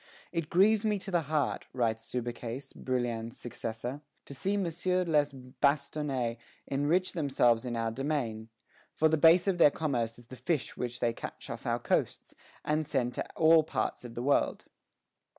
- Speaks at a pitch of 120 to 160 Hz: Yes, medium, 140 Hz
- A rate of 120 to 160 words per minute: No, average, 170 wpm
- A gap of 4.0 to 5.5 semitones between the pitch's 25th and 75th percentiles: Yes, average, 4.9 semitones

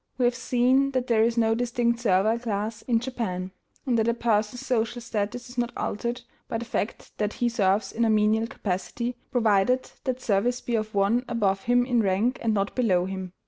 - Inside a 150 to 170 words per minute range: No, average, 200 wpm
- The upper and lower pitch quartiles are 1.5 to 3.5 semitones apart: Yes, average, 2.8 semitones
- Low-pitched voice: No, high, 230 Hz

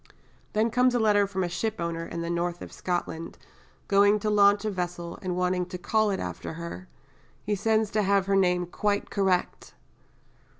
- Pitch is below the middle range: No, high, 190 Hz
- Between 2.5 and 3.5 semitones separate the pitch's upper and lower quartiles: Yes, average, 3.0 semitones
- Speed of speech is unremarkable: Yes, average, 175 wpm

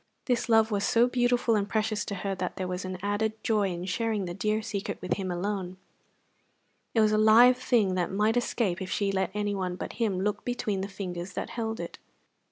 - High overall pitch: Yes, high, 205 Hz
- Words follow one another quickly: Yes, fast, 210 wpm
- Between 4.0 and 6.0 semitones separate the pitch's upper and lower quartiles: No, average, 3.0 semitones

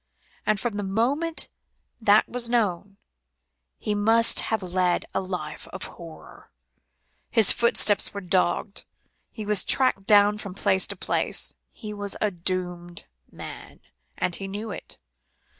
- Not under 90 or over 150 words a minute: Yes, average, 140 wpm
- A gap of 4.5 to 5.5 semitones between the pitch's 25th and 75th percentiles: No, average, 2.9 semitones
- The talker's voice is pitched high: Yes, high, 205 Hz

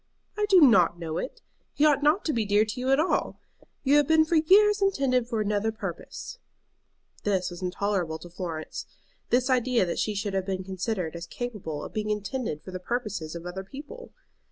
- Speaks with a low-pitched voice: No, high, 215 Hz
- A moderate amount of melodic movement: No, wide, 6.8 semitones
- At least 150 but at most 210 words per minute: Yes, average, 200 wpm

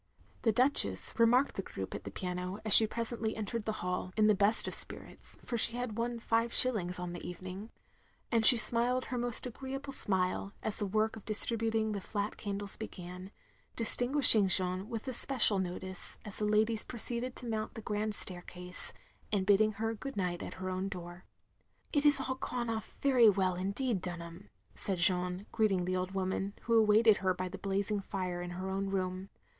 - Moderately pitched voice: No, high, 205 Hz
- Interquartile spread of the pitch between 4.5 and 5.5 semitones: No, average, 3.7 semitones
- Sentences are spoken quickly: No, average, 195 wpm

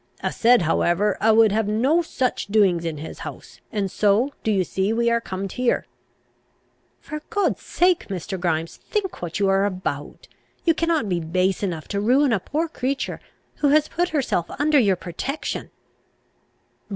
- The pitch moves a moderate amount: No, wide, 7.0 semitones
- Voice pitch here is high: Yes, high, 215 Hz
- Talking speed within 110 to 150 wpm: No, average, 170 wpm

